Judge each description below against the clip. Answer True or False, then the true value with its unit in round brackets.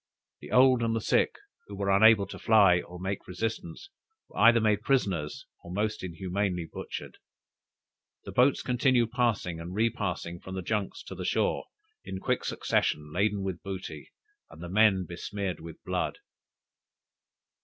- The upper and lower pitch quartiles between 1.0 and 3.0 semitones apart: False (3.8 semitones)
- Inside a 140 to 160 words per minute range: True (155 wpm)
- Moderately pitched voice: False (100 Hz)